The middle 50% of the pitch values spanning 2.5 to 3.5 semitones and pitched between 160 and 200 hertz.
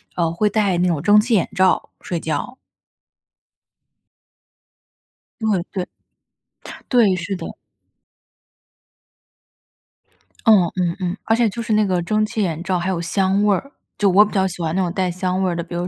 Yes: average, 3.2 semitones; high, 190 Hz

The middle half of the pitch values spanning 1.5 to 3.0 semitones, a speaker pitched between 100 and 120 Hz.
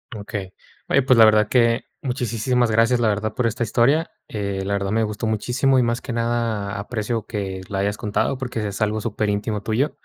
Yes: narrow, 2.6 semitones; low, 110 Hz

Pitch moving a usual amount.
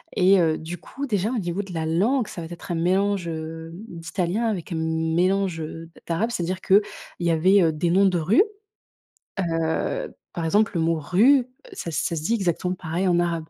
Yes: average, 3.2 semitones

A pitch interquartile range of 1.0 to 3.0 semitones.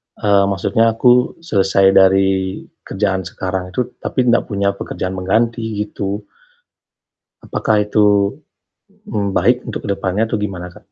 Yes: narrow, 2.4 semitones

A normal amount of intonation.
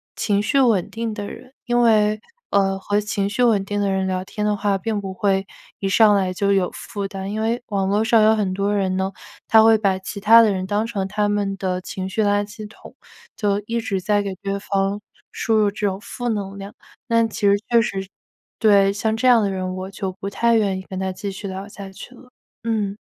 No: narrow, 2.0 semitones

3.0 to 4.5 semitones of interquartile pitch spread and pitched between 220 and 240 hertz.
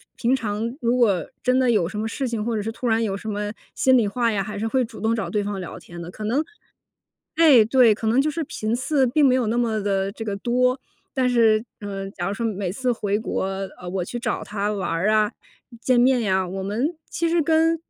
Yes: average, 3.6 semitones; high, 225 Hz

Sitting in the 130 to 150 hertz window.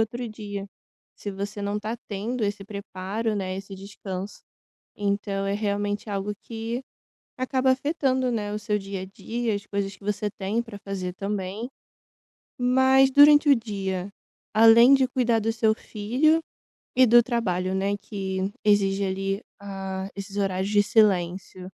No: high, 205 Hz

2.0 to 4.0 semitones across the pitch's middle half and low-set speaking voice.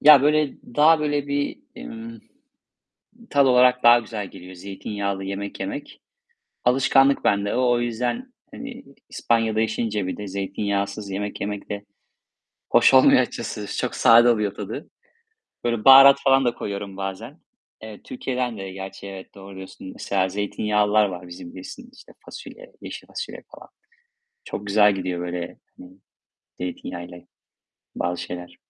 No: average, 4.4 semitones; low, 105 Hz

